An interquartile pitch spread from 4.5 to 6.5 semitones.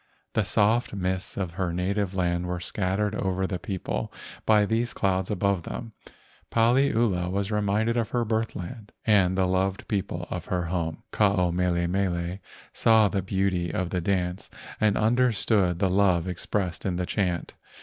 No: average, 2.8 semitones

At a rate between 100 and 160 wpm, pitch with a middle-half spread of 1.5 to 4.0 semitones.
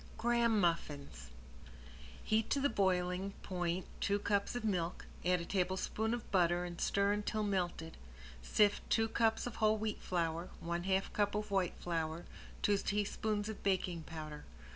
Yes: average, 155 wpm; average, 3.4 semitones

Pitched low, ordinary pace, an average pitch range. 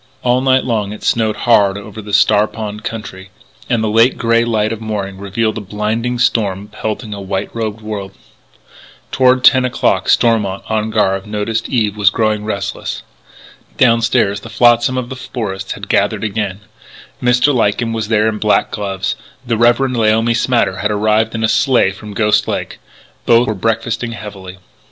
No: low, 110 Hz; average, 170 wpm; narrow, 2.1 semitones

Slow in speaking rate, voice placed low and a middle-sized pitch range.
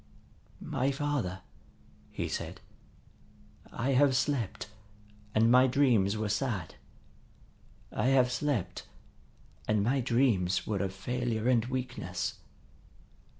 Yes: slow, 105 wpm; low, 120 Hz; average, 4.5 semitones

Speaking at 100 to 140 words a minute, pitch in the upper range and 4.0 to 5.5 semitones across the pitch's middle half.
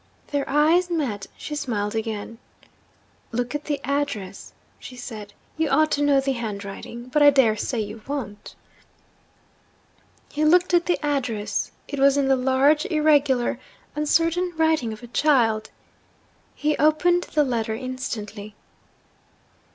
Yes: slow, 135 wpm; very high, 270 Hz; average, 5.1 semitones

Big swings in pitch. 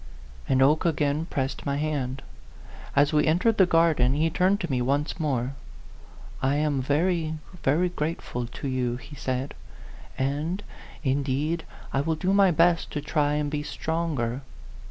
No: average, 3.4 semitones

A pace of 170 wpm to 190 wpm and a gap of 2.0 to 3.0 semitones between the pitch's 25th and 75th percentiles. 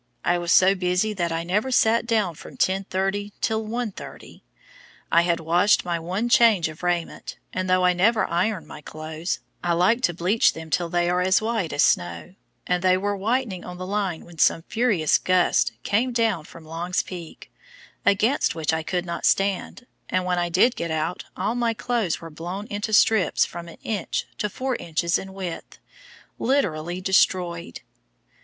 No: average, 180 wpm; average, 3.6 semitones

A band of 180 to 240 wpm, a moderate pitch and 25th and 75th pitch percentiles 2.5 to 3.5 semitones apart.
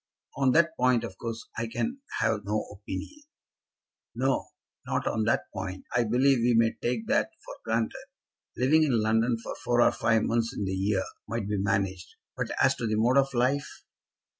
No: average, 185 wpm; low, 115 Hz; average, 3.1 semitones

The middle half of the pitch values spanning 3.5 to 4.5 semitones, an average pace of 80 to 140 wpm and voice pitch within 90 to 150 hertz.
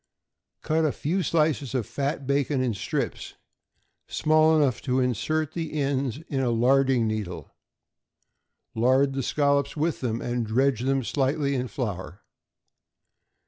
No: average, 3.1 semitones; slow, 135 wpm; low, 135 Hz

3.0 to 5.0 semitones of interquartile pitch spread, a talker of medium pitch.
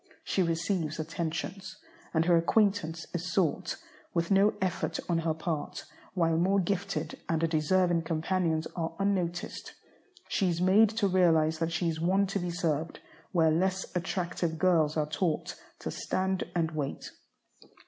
No: narrow, 2.6 semitones; medium, 170 Hz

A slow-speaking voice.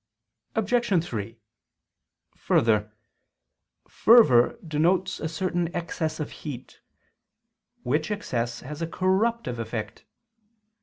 Yes: slow, 90 wpm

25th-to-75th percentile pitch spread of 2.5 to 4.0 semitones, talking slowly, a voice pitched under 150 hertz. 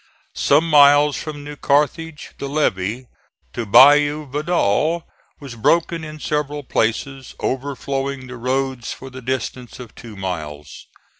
Yes: average, 2.9 semitones; slow, 130 wpm; medium, 140 Hz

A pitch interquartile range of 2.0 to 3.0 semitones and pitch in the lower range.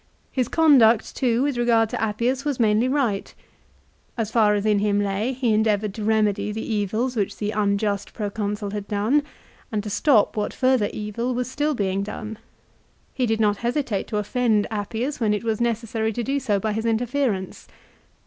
No: average, 2.7 semitones; high, 220 Hz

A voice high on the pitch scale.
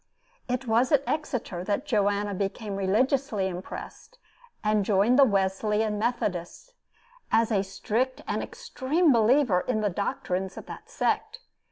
Yes: high, 215 Hz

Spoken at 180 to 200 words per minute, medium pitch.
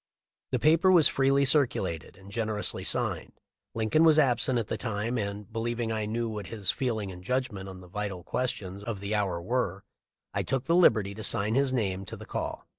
No: average, 195 wpm; low, 110 Hz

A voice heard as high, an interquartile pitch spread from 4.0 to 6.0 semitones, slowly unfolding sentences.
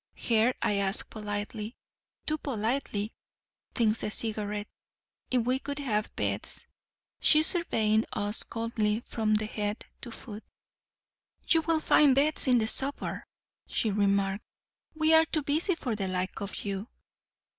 Yes: high, 220 Hz; average, 4.7 semitones; slow, 130 wpm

